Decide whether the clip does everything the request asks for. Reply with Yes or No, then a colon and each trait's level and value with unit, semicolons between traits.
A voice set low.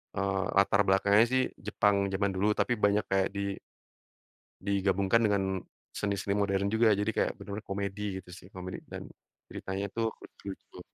Yes: low, 100 Hz